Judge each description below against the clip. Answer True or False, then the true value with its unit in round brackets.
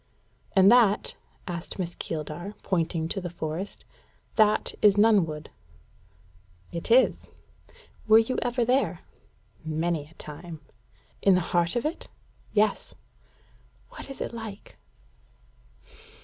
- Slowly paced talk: True (115 wpm)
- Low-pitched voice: False (190 Hz)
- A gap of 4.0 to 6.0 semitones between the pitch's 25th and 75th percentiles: True (5.1 semitones)